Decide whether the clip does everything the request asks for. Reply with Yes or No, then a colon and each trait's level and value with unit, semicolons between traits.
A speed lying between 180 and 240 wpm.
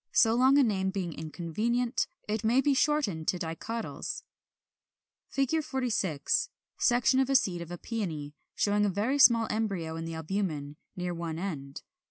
No: average, 165 wpm